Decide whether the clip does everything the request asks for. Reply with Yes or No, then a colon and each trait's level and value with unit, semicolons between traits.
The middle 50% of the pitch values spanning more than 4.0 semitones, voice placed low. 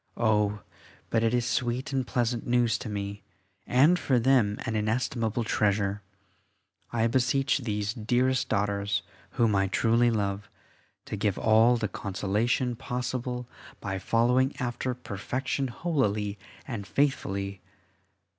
No: average, 3.3 semitones; low, 115 Hz